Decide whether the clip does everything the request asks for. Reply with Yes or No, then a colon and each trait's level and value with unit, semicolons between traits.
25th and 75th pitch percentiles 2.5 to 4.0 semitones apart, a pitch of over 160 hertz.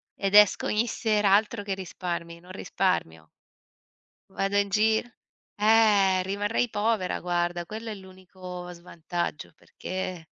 Yes: average, 2.8 semitones; high, 190 Hz